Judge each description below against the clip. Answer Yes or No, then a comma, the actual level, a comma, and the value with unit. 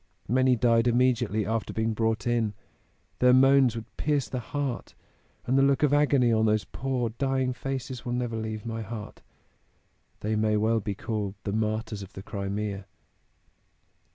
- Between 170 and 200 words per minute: No, average, 160 wpm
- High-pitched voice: No, low, 115 Hz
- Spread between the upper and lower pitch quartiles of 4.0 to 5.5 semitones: No, average, 3.0 semitones